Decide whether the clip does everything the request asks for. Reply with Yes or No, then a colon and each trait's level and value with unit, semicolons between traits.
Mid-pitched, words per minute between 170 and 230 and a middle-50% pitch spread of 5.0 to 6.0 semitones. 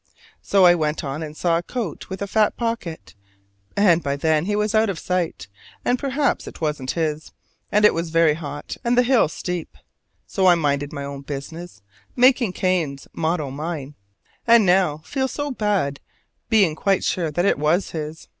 Yes: medium, 170 Hz; average, 185 wpm; wide, 5.4 semitones